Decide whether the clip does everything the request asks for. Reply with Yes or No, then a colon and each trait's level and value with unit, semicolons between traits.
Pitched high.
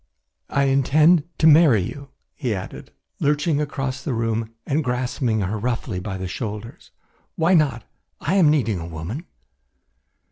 No: low, 130 Hz